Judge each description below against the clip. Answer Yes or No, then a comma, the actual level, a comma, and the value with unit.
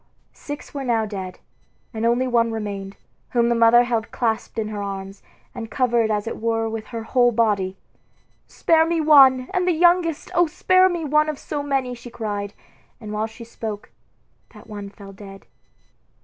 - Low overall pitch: No, high, 230 Hz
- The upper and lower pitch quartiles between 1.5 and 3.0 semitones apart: No, average, 4.4 semitones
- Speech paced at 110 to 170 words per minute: No, average, 180 wpm